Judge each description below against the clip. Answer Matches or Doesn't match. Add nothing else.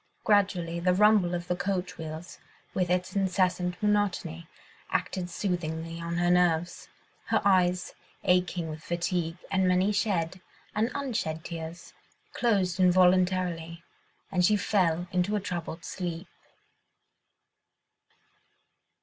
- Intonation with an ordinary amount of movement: Doesn't match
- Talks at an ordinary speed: Doesn't match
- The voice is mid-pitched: Matches